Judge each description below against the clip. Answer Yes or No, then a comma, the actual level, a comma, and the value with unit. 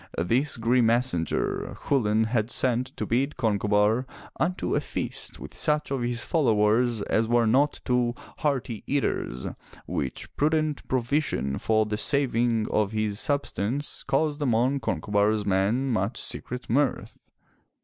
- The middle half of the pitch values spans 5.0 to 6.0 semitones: No, average, 4.1 semitones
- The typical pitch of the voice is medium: No, low, 120 Hz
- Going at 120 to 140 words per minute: Yes, slow, 135 wpm